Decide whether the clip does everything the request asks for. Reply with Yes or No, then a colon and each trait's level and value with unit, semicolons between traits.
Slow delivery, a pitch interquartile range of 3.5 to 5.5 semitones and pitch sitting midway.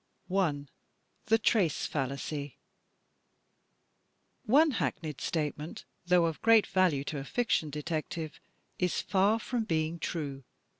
Yes: slow, 110 wpm; average, 5.0 semitones; medium, 165 Hz